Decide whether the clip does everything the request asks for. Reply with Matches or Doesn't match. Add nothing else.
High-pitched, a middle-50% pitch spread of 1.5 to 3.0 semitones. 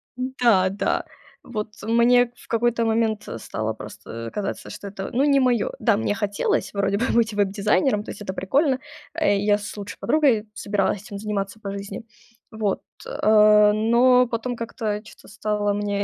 Matches